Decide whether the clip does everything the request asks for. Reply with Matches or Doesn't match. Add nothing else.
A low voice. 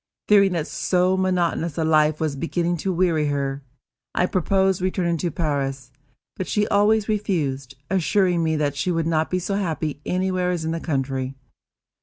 Doesn't match